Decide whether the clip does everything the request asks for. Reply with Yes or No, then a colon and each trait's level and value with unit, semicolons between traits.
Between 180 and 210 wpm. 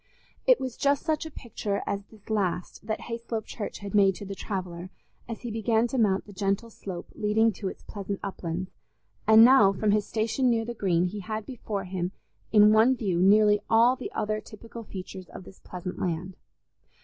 Yes: average, 195 wpm